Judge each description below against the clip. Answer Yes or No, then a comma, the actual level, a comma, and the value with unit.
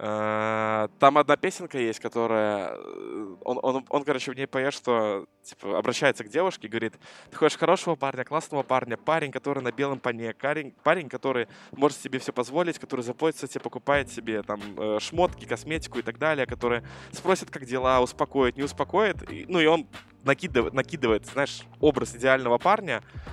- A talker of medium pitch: No, low, 130 Hz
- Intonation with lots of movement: No, average, 3.9 semitones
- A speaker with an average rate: No, fast, 165 wpm